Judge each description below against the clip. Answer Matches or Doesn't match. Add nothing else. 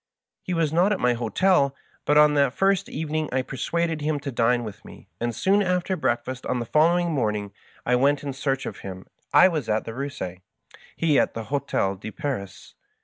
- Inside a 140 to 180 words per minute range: Doesn't match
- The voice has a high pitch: Doesn't match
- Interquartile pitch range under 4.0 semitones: Doesn't match